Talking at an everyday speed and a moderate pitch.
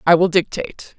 Yes: average, 185 wpm; medium, 170 Hz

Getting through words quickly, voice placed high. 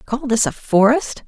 No: average, 190 wpm; high, 240 Hz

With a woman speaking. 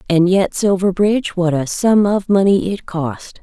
Yes: female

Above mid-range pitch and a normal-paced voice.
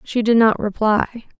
Yes: high, 220 Hz; average, 170 wpm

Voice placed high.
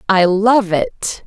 Yes: high, 210 Hz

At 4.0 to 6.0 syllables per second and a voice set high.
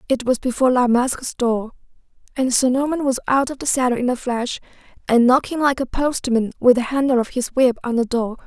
Yes: 5.6 syllables/s; very high, 250 Hz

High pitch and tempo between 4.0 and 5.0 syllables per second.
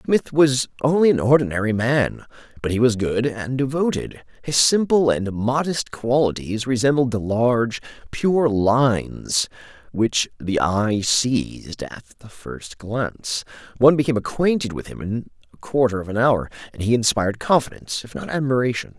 No: low, 120 Hz; 4.8 syllables/s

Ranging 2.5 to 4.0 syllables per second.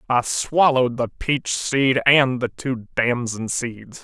Yes: 3.6 syllables/s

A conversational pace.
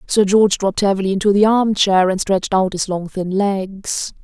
No: fast, 210 wpm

